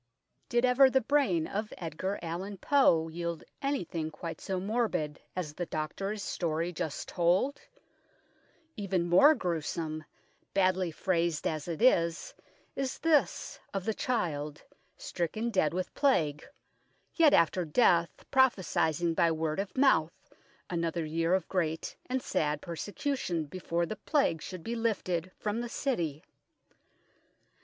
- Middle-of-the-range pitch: Yes, medium, 175 Hz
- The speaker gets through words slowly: Yes, slow, 130 wpm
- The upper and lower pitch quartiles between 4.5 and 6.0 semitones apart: Yes, average, 5.1 semitones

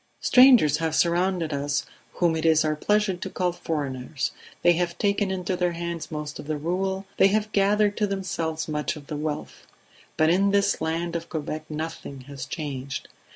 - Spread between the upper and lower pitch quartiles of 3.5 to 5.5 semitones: Yes, average, 4.0 semitones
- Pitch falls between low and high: Yes, medium, 165 Hz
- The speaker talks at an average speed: Yes, average, 180 wpm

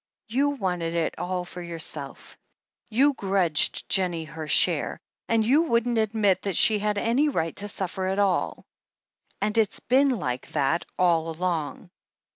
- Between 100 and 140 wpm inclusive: No, average, 155 wpm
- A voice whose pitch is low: No, high, 190 Hz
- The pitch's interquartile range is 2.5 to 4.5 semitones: No, average, 4.9 semitones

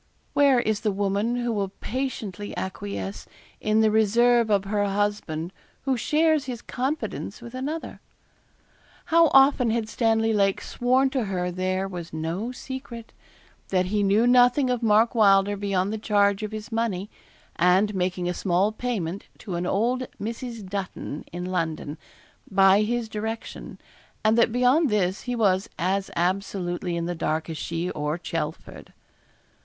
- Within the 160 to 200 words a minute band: No, average, 150 wpm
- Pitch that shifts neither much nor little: Yes, average, 4.3 semitones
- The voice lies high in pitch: Yes, high, 205 Hz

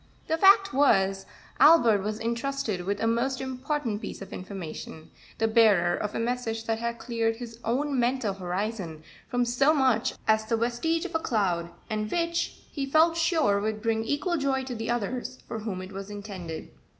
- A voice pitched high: Yes, high, 230 Hz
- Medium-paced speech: Yes, average, 180 wpm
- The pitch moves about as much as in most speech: Yes, average, 4.5 semitones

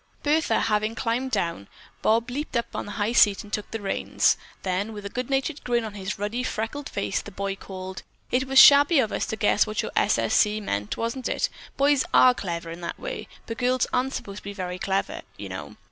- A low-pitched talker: No, high, 220 Hz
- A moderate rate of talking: No, fast, 220 wpm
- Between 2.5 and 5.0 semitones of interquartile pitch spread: Yes, average, 4.2 semitones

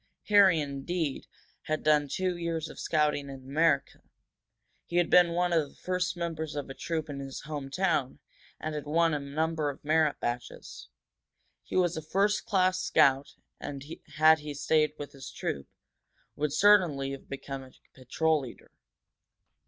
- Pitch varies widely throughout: No, average, 3.3 semitones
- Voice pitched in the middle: Yes, medium, 155 Hz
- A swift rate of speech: No, average, 160 wpm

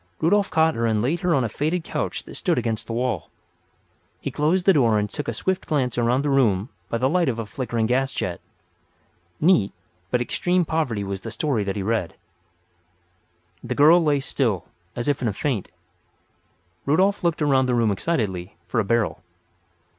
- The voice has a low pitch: Yes, low, 125 Hz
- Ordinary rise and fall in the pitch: No, wide, 5.7 semitones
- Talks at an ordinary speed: Yes, average, 190 wpm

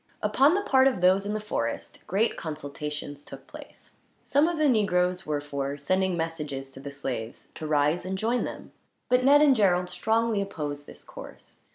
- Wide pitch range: Yes, wide, 7.3 semitones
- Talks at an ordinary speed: Yes, average, 185 wpm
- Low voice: No, medium, 180 Hz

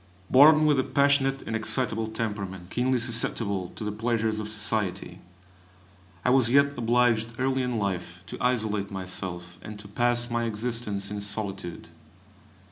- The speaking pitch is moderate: No, low, 110 Hz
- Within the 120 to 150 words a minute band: Yes, average, 145 wpm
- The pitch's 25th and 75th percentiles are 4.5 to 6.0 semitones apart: No, average, 3.5 semitones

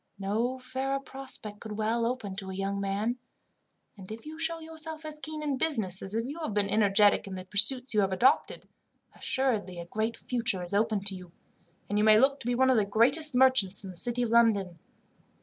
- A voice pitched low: No, high, 225 Hz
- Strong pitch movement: No, average, 4.8 semitones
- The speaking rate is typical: No, fast, 210 wpm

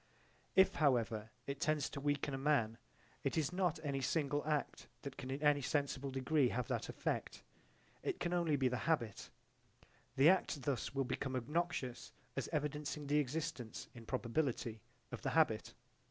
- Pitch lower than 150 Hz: Yes, medium, 140 Hz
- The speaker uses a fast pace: No, average, 165 wpm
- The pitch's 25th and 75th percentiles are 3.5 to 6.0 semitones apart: No, average, 3.0 semitones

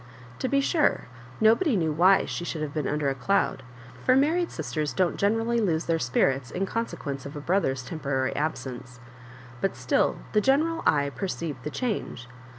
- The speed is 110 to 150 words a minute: No, average, 175 wpm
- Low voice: No, medium, 165 Hz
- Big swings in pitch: Yes, wide, 8.2 semitones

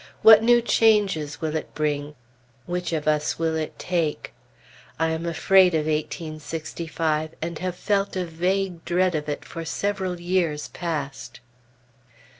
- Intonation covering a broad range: No, average, 3.1 semitones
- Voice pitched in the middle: Yes, medium, 165 Hz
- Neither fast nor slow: Yes, average, 150 wpm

